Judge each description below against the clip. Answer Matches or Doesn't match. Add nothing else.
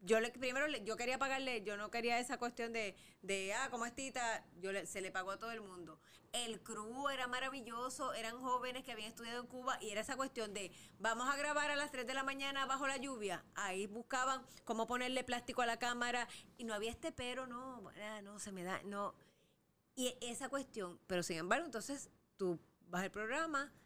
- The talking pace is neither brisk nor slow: Doesn't match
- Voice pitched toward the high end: Matches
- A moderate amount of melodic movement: Matches